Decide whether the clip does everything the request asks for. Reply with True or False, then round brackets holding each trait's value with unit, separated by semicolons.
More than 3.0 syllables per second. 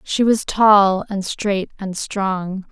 False (2.8 syllables/s)